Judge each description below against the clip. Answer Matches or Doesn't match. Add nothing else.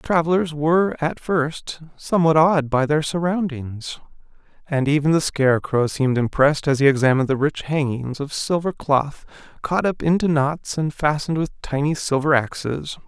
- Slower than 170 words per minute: Matches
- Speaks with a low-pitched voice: Doesn't match